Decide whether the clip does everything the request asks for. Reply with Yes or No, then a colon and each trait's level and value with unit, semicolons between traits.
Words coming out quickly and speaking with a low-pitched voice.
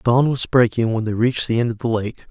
Yes: fast, 285 wpm; low, 120 Hz